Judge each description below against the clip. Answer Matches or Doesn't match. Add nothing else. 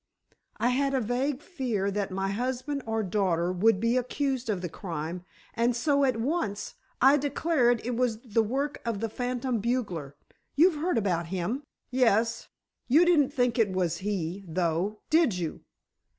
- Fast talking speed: Doesn't match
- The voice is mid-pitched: Doesn't match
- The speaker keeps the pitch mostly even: Doesn't match